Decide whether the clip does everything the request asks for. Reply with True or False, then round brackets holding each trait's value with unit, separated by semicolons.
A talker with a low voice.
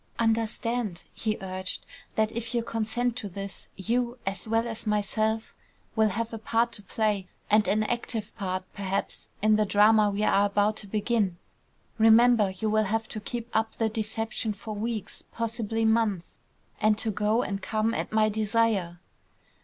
False (215 Hz)